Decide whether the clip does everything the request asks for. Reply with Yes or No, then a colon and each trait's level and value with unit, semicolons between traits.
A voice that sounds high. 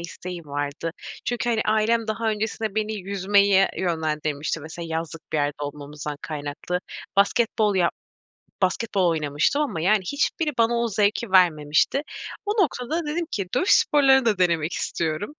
Yes: high, 195 Hz